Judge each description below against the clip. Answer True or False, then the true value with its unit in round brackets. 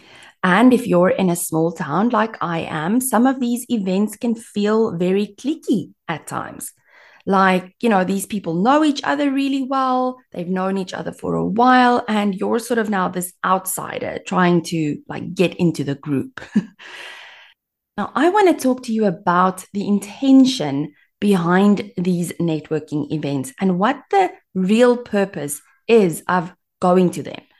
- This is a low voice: False (200 Hz)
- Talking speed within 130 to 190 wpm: True (165 wpm)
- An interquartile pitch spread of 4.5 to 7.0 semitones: True (5.4 semitones)